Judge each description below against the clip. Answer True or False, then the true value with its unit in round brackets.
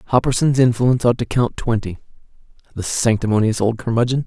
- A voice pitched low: True (115 Hz)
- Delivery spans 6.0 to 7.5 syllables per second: True (6.2 syllables/s)